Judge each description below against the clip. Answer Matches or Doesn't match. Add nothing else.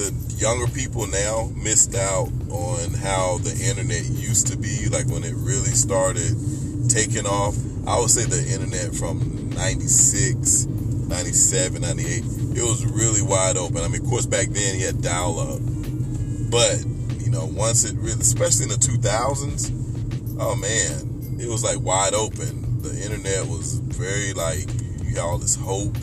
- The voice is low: Matches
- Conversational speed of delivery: Matches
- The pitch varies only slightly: Matches